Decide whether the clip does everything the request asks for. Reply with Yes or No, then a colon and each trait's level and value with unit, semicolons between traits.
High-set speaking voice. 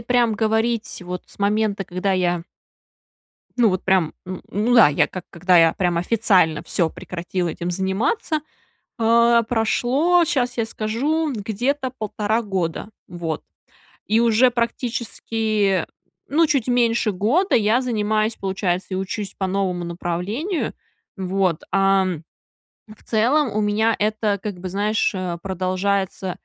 Yes: high, 210 Hz